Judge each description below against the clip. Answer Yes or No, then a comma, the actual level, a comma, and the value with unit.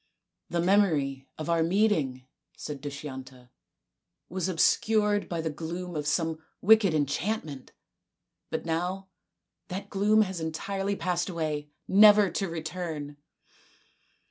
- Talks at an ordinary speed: No, slow, 125 wpm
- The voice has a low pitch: No, medium, 170 Hz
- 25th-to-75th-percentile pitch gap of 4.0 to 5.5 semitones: Yes, average, 4.6 semitones